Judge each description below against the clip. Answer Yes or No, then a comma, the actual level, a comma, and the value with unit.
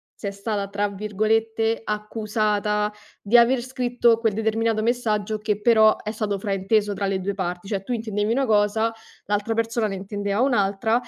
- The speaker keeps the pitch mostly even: Yes, narrow, 1.9 semitones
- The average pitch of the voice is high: Yes, high, 215 Hz